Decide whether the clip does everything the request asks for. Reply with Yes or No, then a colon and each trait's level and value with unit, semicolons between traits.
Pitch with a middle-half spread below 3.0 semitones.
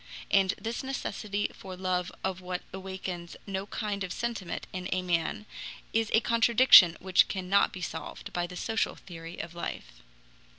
Yes: narrow, 2.5 semitones